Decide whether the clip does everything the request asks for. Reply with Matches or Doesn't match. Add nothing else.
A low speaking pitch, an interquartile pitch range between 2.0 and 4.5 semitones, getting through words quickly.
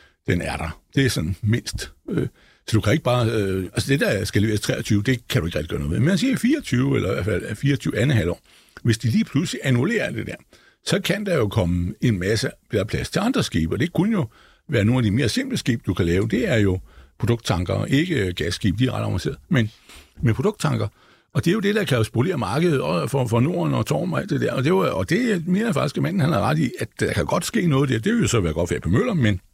Doesn't match